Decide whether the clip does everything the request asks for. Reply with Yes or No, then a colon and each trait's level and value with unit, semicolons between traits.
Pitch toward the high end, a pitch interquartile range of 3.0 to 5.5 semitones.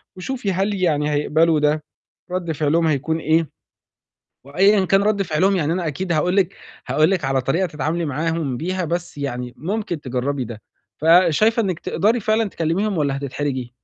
No: medium, 165 Hz; average, 4.4 semitones